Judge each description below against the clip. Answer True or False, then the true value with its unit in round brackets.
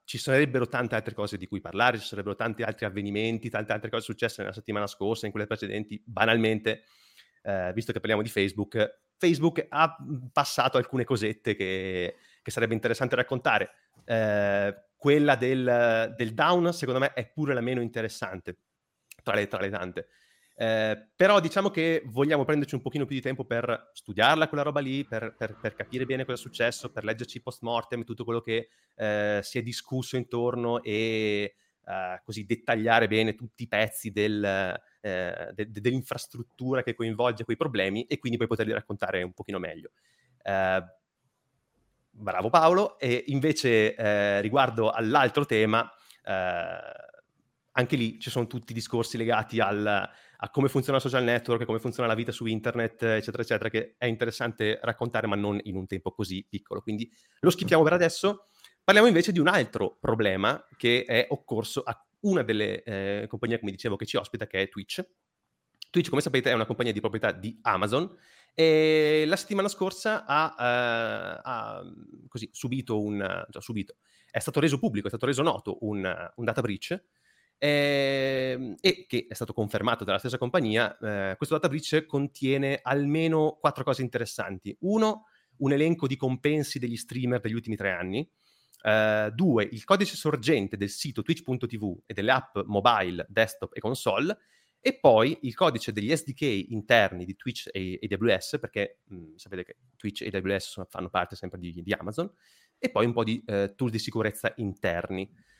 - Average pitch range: True (4.2 semitones)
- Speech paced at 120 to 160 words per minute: False (170 wpm)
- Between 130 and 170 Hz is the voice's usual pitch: False (115 Hz)